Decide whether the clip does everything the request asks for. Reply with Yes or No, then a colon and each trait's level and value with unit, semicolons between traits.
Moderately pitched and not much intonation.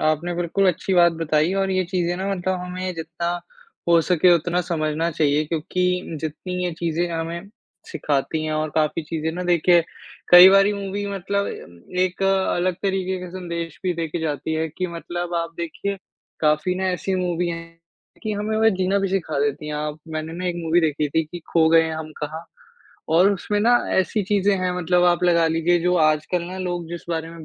Yes: medium, 175 Hz; narrow, 2.3 semitones